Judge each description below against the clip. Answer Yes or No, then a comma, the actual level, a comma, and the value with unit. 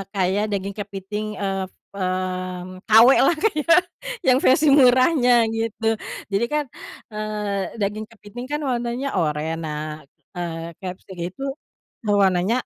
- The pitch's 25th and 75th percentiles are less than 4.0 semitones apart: No, average, 4.5 semitones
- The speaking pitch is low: No, high, 200 Hz